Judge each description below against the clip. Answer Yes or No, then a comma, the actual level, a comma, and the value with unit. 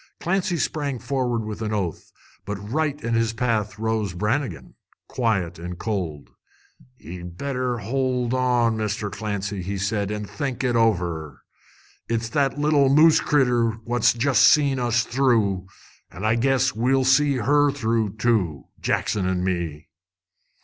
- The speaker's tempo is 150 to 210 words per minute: No, average, 140 wpm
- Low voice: Yes, low, 115 Hz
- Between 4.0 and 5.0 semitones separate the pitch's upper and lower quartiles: Yes, average, 4.6 semitones